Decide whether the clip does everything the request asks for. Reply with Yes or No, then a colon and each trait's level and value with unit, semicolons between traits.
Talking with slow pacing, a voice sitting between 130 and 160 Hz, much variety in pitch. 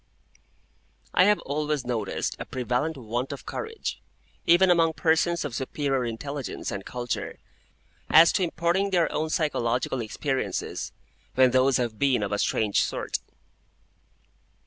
No: slow, 130 wpm; medium, 140 Hz; average, 5.0 semitones